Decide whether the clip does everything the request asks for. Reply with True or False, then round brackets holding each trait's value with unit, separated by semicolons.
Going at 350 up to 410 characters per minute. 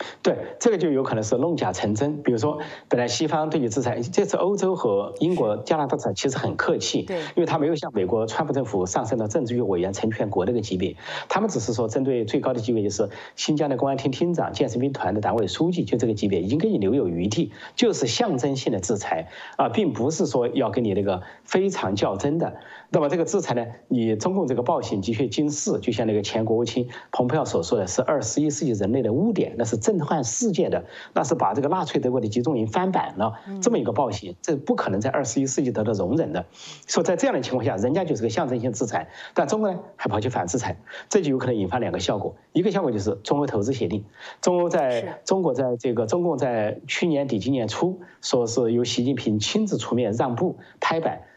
True (355 characters per minute)